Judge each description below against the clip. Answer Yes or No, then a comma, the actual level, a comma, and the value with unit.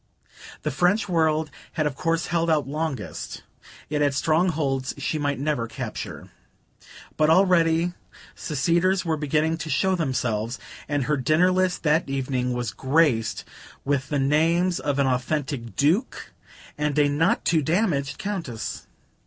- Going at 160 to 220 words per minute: No, average, 140 wpm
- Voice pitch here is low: No, medium, 150 Hz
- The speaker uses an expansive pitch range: No, average, 3.4 semitones